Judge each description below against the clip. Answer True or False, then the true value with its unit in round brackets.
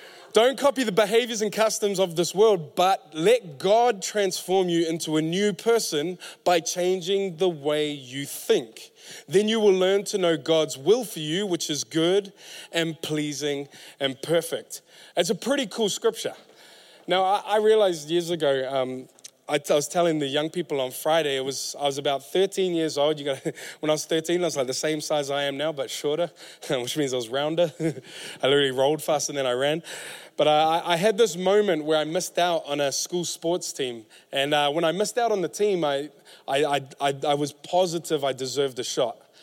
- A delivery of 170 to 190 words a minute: False (205 wpm)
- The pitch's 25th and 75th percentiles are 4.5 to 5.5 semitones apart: True (4.8 semitones)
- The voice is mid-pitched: True (165 Hz)